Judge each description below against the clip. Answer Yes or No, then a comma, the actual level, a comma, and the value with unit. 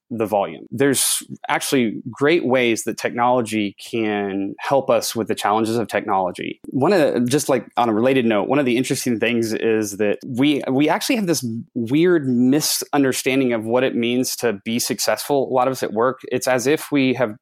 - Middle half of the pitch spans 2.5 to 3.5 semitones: Yes, average, 2.9 semitones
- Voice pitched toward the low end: Yes, low, 125 Hz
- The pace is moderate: Yes, average, 195 wpm